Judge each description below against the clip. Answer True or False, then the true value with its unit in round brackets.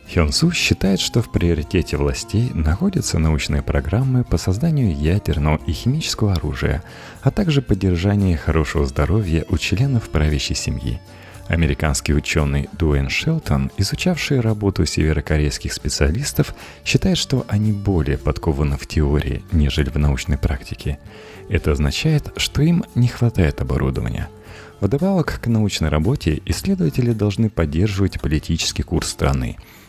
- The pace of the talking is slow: False (120 wpm)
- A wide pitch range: True (6.7 semitones)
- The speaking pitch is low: True (90 Hz)